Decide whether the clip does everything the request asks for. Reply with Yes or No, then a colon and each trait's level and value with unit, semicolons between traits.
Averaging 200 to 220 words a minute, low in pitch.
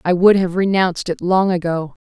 No: fast, 205 wpm; medium, 180 Hz